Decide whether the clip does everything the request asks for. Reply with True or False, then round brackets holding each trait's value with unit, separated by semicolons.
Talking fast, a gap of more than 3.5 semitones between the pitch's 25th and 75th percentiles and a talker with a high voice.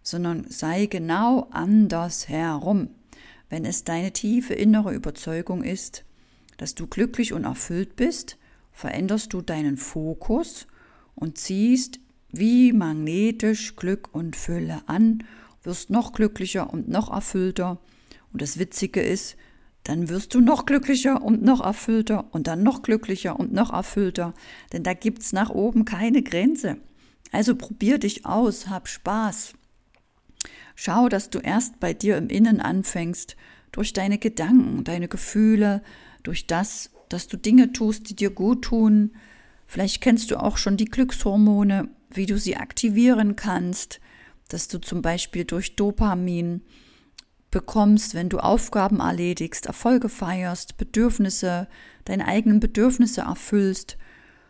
False (135 wpm; 4.0 semitones; 210 Hz)